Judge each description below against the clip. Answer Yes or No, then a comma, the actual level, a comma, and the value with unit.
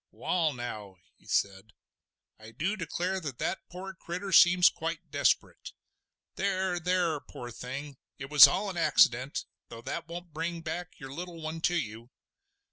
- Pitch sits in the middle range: Yes, medium, 165 Hz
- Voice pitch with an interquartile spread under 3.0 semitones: No, average, 5.0 semitones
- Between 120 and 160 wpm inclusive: Yes, average, 150 wpm